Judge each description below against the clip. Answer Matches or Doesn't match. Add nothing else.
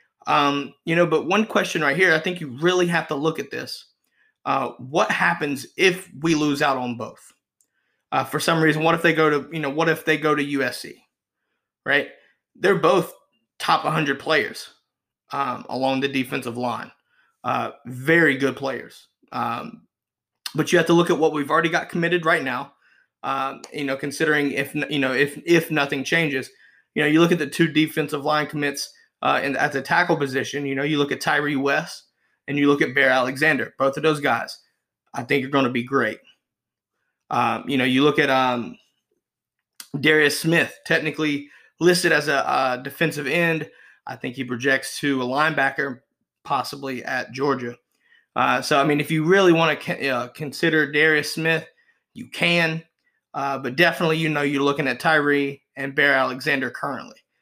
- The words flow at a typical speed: Matches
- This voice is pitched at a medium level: Matches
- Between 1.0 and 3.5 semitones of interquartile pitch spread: Matches